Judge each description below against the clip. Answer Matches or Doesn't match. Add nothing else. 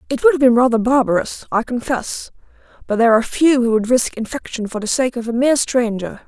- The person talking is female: Matches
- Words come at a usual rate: Doesn't match